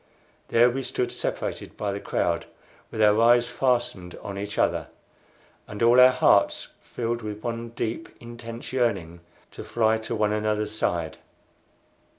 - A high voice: No, low, 115 Hz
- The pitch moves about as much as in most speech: No, narrow, 2.3 semitones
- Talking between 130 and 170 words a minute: Yes, average, 150 wpm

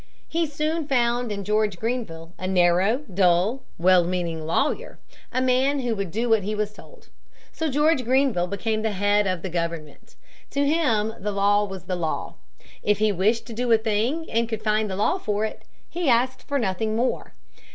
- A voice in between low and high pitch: No, high, 215 Hz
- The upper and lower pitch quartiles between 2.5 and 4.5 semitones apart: No, average, 5.0 semitones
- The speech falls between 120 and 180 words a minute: No, average, 190 wpm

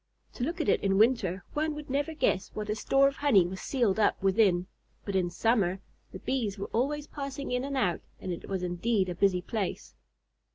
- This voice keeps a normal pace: No, fast, 210 wpm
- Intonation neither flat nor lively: No, wide, 6.4 semitones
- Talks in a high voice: Yes, high, 215 Hz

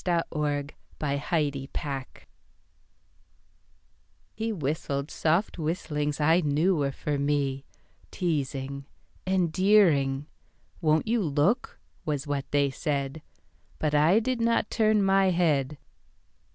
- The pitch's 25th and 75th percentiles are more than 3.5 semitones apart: Yes, average, 4.3 semitones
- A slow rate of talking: Yes, slow, 100 wpm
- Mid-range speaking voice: Yes, medium, 150 Hz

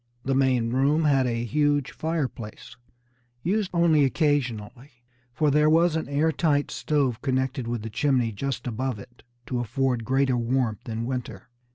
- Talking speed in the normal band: Yes, average, 155 wpm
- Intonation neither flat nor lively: Yes, average, 3.5 semitones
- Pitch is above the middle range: No, low, 130 Hz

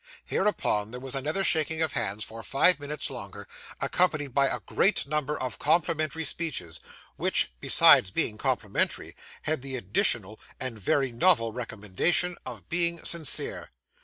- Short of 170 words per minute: Yes, average, 140 wpm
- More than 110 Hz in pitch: Yes, medium, 140 Hz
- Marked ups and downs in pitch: Yes, wide, 5.9 semitones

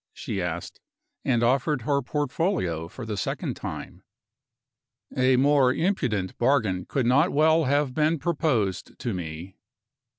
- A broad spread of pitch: Yes, wide, 6.7 semitones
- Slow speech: Yes, slow, 130 wpm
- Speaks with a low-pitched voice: Yes, low, 130 Hz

